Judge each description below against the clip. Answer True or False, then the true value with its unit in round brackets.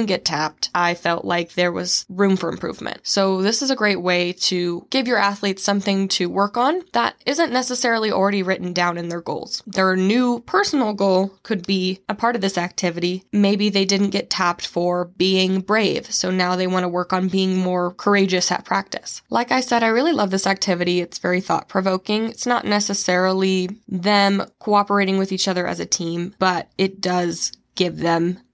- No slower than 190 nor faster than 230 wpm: True (195 wpm)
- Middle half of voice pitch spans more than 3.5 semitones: False (2.4 semitones)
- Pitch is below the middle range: False (190 Hz)